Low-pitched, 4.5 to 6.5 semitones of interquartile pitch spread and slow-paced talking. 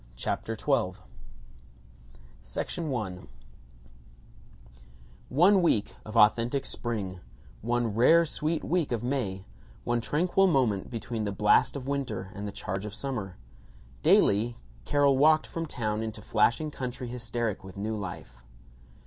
Yes: low, 115 Hz; wide, 5.6 semitones; slow, 120 wpm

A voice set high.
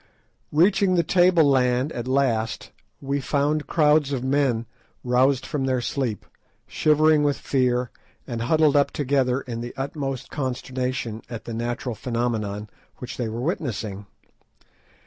No: low, 130 Hz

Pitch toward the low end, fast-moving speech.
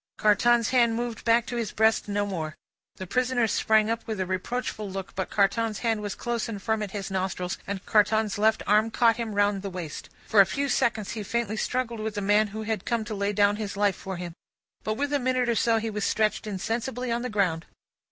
No: high, 215 Hz; fast, 230 wpm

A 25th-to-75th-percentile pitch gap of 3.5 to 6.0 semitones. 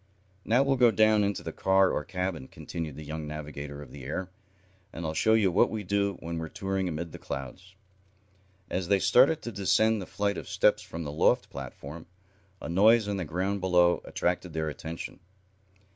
Yes: average, 4.2 semitones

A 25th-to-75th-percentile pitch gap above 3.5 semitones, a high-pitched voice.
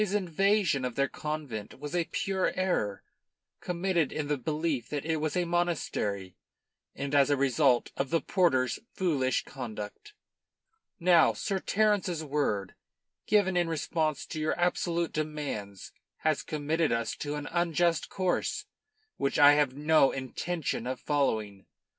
No: average, 4.5 semitones; medium, 155 Hz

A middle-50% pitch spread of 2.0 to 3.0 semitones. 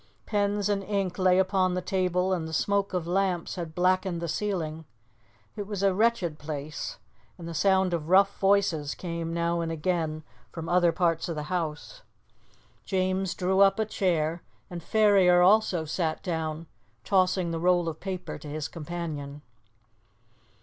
Yes: average, 2.7 semitones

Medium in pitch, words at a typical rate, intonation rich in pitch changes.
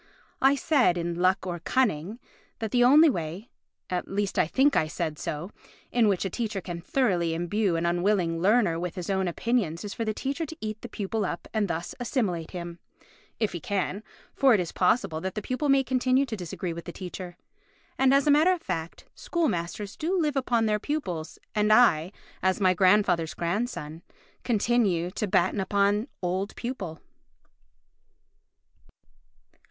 No: high, 200 Hz; average, 170 wpm; wide, 5.7 semitones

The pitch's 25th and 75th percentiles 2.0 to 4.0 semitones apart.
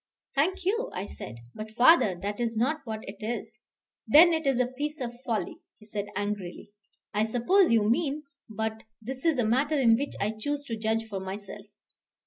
No: average, 5.1 semitones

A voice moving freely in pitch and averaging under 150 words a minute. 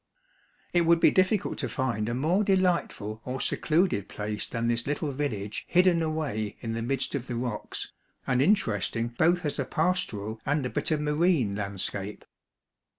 No: wide, 7.0 semitones; average, 165 wpm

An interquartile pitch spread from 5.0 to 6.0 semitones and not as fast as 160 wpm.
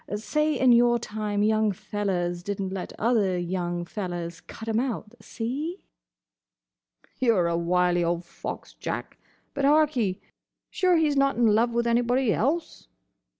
Yes: wide, 5.6 semitones; average, 150 wpm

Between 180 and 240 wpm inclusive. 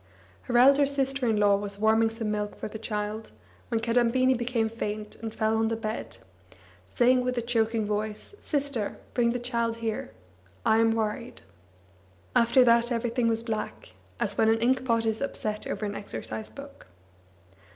No: average, 165 wpm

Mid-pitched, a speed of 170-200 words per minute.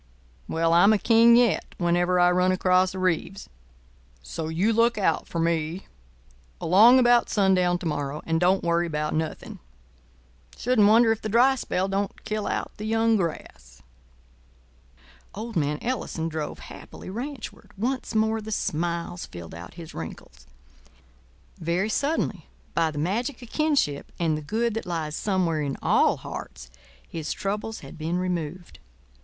No: medium, 180 Hz; average, 150 wpm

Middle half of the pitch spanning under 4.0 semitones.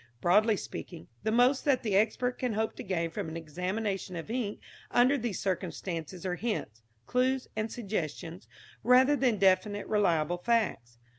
No: average, 5.2 semitones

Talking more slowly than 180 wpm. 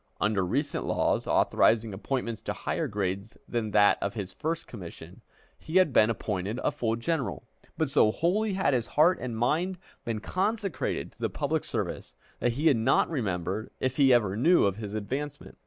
No: average, 185 wpm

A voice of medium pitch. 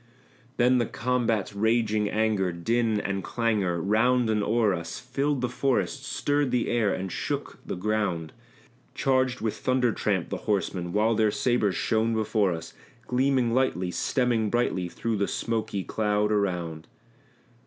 No: low, 110 Hz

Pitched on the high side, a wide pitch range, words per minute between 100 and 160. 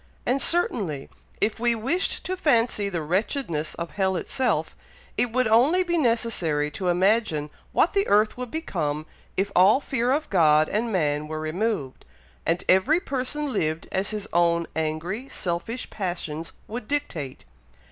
Yes: high, 200 Hz; wide, 7.2 semitones; average, 150 wpm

